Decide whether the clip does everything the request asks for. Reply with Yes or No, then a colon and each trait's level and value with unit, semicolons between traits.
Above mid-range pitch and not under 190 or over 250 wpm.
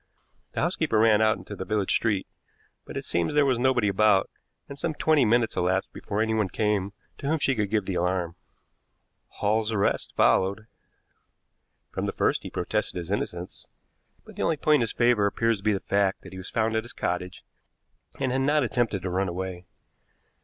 No: low, 105 Hz; average, 195 wpm